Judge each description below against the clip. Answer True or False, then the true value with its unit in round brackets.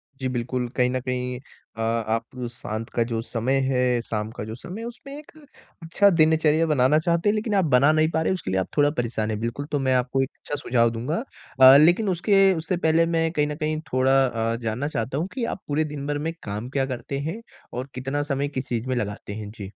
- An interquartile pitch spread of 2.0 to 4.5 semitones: False (5.0 semitones)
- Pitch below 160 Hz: True (135 Hz)